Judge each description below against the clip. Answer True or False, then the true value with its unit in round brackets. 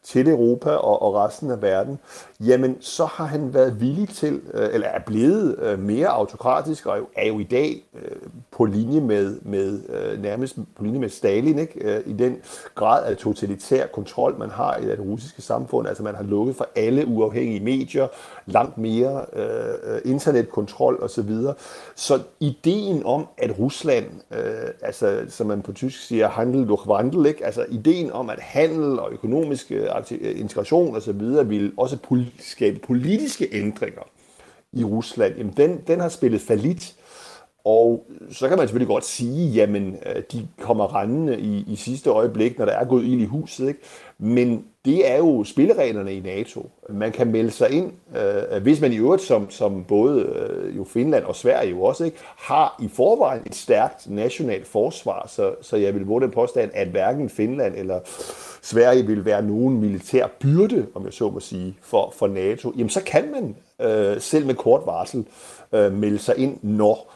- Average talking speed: True (175 wpm)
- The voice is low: True (130 Hz)